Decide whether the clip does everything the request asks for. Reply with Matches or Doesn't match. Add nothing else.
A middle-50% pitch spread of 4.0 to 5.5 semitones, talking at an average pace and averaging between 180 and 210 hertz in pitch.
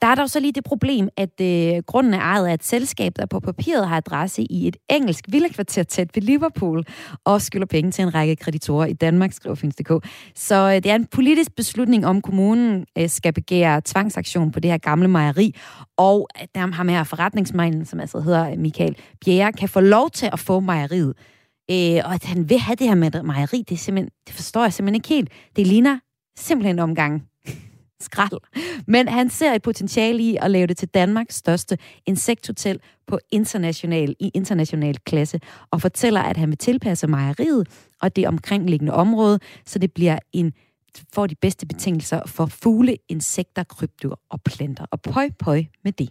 Matches